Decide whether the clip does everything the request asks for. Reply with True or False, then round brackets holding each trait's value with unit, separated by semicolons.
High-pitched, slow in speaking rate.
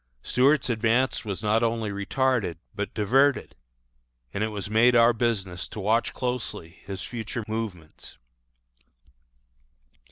False (110 Hz; 120 wpm)